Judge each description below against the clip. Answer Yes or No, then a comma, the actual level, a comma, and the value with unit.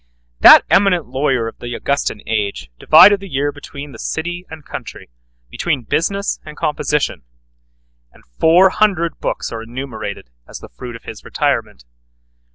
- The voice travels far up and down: Yes, wide, 6.6 semitones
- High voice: No, medium, 145 Hz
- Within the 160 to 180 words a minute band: No, average, 150 wpm